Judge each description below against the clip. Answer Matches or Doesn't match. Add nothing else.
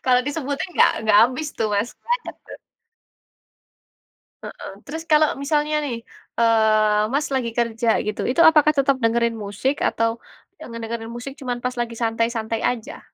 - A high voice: Matches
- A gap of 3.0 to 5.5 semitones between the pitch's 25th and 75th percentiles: Matches